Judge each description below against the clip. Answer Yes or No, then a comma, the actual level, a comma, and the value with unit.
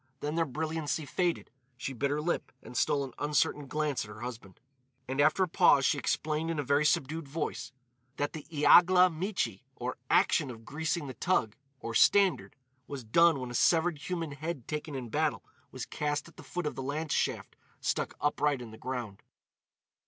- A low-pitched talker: No, medium, 145 Hz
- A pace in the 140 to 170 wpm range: No, average, 190 wpm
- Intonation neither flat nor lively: Yes, average, 3.7 semitones